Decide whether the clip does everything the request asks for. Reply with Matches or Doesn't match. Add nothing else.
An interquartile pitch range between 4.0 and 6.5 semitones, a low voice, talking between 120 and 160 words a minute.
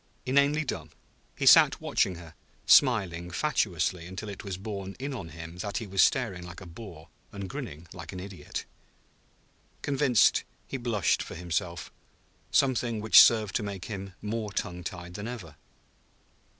Matches